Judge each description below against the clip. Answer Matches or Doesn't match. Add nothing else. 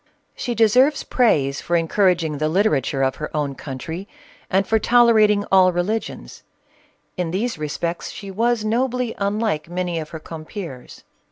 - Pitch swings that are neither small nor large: Doesn't match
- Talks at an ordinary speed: Matches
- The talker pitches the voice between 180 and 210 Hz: Matches